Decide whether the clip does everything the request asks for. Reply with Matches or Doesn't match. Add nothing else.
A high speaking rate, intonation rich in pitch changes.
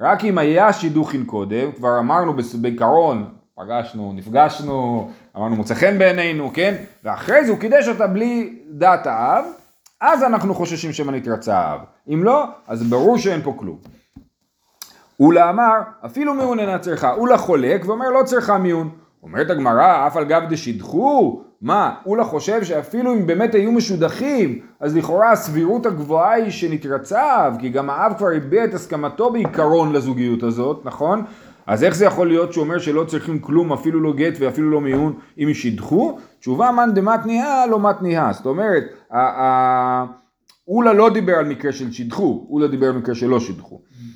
Matches